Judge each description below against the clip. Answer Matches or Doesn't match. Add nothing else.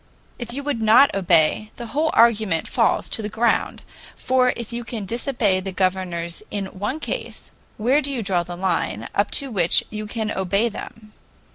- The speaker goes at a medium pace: Matches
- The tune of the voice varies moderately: Matches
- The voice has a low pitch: Doesn't match